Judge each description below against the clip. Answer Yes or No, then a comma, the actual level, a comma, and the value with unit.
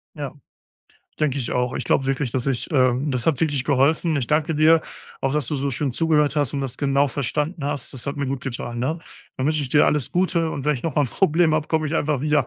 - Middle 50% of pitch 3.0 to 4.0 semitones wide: No, narrow, 2.6 semitones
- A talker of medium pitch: Yes, medium, 145 Hz